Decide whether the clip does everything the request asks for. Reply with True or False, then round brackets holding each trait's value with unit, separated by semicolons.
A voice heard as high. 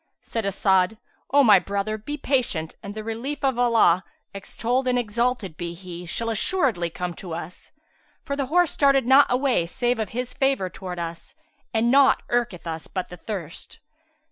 True (220 Hz)